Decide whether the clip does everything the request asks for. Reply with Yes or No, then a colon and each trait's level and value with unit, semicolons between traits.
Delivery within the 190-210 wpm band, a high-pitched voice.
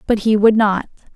Yes: fast, 205 wpm; high, 210 Hz